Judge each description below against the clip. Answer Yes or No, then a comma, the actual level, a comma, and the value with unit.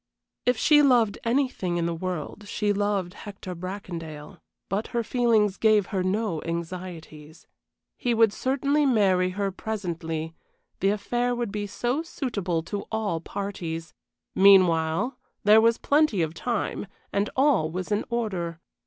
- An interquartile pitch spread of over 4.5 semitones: Yes, average, 4.9 semitones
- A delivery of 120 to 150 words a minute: Yes, average, 140 wpm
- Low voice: No, high, 200 Hz